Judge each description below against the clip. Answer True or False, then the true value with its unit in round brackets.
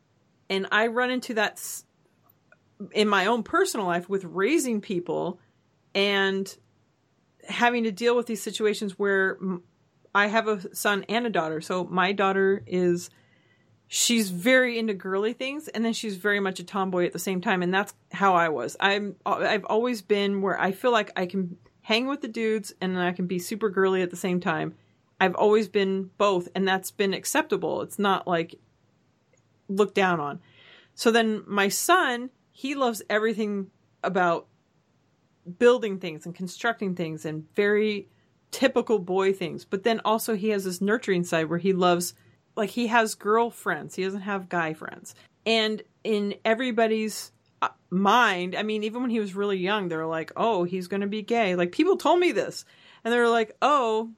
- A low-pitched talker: False (200 Hz)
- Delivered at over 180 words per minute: False (175 wpm)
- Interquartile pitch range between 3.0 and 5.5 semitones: True (3.5 semitones)